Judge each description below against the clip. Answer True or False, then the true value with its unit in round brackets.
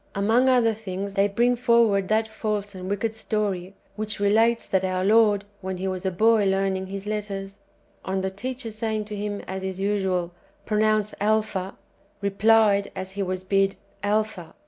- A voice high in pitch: True (205 Hz)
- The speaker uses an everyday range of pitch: False (2.3 semitones)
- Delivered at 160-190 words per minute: True (170 wpm)